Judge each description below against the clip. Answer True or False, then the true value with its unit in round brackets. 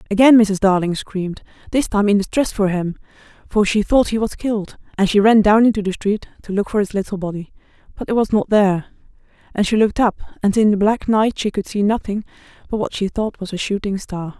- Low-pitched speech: False (205 Hz)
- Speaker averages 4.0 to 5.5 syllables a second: False (6.0 syllables/s)